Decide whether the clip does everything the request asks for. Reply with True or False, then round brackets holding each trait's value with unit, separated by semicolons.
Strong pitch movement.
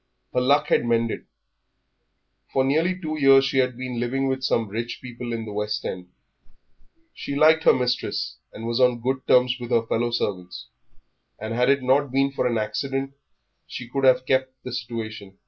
False (2.6 semitones)